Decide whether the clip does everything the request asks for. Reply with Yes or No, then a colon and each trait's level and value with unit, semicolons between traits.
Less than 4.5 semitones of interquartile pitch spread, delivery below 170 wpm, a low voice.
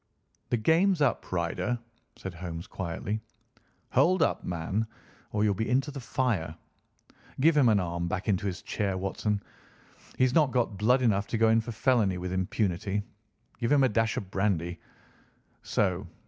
No: average, 4.8 semitones; average, 160 wpm; low, 105 Hz